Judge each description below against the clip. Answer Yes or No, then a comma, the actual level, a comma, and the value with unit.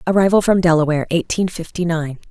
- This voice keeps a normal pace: Yes, average, 155 wpm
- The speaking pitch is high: No, medium, 170 Hz